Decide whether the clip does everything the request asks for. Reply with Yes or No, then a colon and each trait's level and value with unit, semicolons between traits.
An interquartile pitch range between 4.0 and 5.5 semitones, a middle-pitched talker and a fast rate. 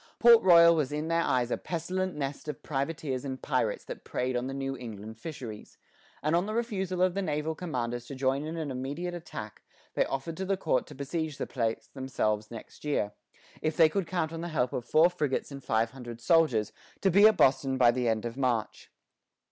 Yes: average, 5.1 semitones; medium, 145 Hz; fast, 210 wpm